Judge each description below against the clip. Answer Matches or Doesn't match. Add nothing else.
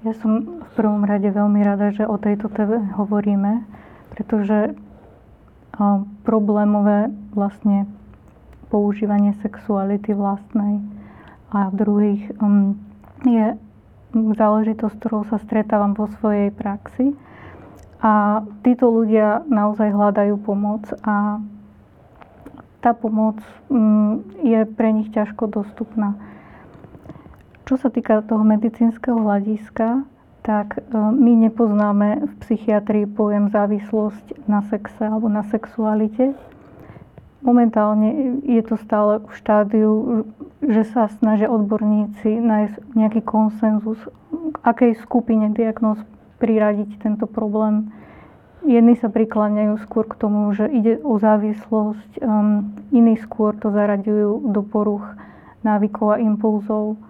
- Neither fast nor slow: Doesn't match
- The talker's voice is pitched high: Matches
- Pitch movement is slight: Matches